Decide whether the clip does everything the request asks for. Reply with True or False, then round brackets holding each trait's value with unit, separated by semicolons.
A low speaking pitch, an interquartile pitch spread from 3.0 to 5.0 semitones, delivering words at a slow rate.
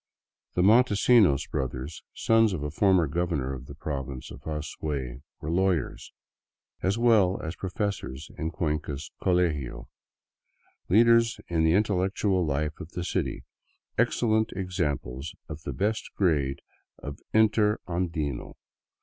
False (85 Hz; 5.6 semitones; 125 wpm)